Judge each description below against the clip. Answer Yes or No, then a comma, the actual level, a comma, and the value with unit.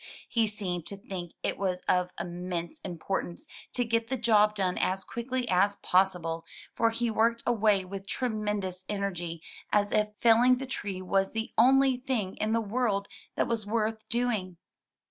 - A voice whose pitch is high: Yes, high, 210 Hz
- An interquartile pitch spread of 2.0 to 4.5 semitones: Yes, average, 3.7 semitones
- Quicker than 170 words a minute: No, average, 165 wpm